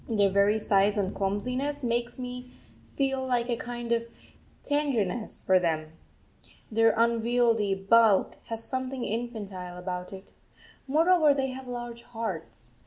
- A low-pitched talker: No, high, 230 Hz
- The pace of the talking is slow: Yes, slow, 125 wpm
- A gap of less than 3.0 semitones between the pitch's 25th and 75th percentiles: No, average, 3.9 semitones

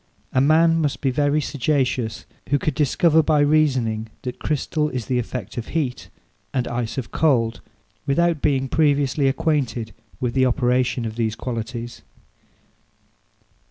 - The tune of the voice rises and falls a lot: No, average, 3.8 semitones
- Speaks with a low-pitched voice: Yes, low, 130 Hz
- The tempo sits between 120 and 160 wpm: Yes, average, 140 wpm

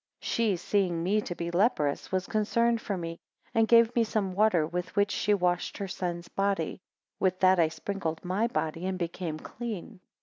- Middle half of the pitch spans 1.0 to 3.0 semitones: No, average, 3.6 semitones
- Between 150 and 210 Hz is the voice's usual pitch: Yes, high, 190 Hz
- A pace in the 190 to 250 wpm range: Yes, average, 195 wpm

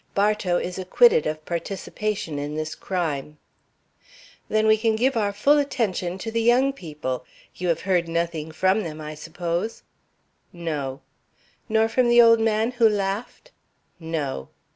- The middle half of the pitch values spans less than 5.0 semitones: No, wide, 5.6 semitones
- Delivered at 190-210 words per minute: No, average, 145 wpm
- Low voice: No, high, 190 Hz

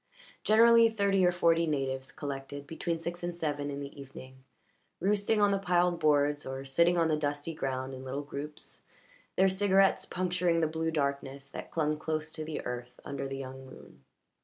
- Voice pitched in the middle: Yes, medium, 155 Hz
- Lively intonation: No, average, 4.2 semitones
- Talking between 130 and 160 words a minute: No, average, 180 wpm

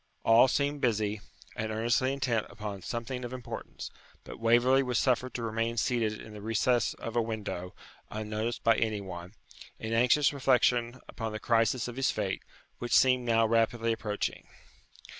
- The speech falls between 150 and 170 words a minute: Yes, average, 160 wpm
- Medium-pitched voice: No, low, 115 Hz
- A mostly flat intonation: Yes, narrow, 2.3 semitones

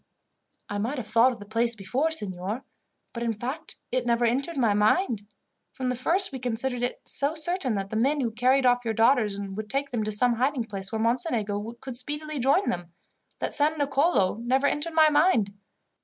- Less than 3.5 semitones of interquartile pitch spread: No, average, 4.4 semitones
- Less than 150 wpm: No, average, 200 wpm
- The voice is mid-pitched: No, high, 245 Hz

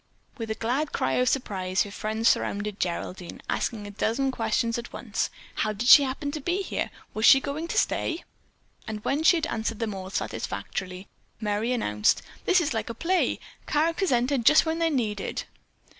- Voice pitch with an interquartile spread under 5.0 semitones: No, wide, 5.5 semitones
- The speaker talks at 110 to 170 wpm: No, average, 185 wpm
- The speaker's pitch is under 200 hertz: No, high, 230 Hz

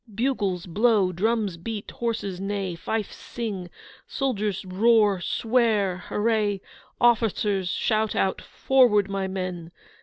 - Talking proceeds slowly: Yes, slow, 110 wpm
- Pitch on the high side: Yes, high, 205 Hz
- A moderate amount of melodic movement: Yes, average, 3.2 semitones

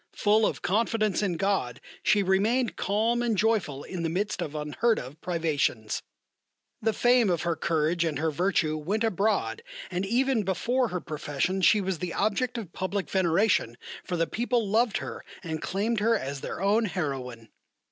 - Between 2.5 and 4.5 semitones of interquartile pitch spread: No, average, 5.2 semitones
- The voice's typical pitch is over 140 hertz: Yes, high, 190 Hz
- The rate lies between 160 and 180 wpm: Yes, average, 170 wpm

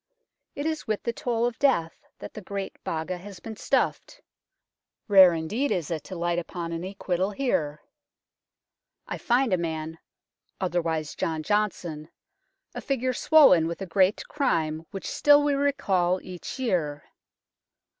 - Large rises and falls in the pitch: Yes, wide, 6.2 semitones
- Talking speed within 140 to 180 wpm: Yes, average, 150 wpm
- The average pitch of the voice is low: No, medium, 185 Hz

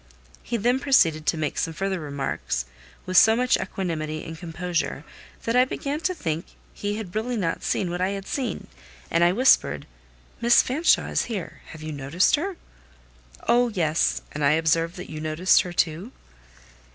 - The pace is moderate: Yes, average, 170 wpm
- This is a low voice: No, medium, 180 Hz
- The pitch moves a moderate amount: No, wide, 6.7 semitones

